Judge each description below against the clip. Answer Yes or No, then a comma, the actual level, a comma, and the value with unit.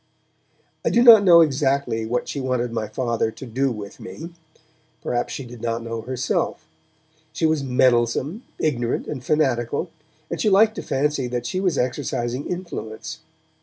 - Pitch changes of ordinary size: Yes, average, 4.4 semitones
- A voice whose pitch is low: Yes, low, 130 Hz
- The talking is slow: No, average, 160 wpm